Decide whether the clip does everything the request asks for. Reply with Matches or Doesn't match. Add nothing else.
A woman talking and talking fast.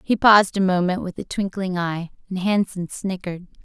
Doesn't match